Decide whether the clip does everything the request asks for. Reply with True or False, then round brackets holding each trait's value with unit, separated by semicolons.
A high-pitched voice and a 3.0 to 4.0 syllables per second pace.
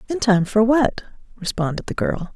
False (210 Hz; 5.0 syllables/s)